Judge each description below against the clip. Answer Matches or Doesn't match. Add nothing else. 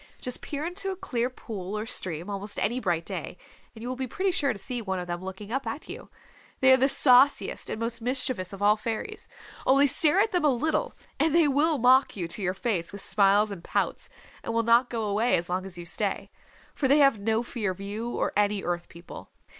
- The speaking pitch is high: Matches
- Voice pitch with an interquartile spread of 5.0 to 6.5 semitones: Matches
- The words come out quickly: Matches